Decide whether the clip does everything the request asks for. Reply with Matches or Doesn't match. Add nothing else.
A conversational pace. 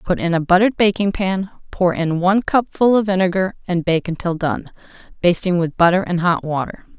Matches